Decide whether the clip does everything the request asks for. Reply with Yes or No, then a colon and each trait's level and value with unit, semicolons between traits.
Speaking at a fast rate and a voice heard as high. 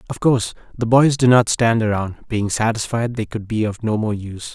No: fast, 225 wpm; low, 110 Hz